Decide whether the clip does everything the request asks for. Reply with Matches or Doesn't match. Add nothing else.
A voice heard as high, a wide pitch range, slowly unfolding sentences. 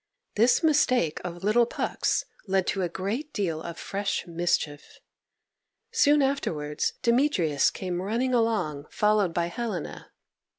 Matches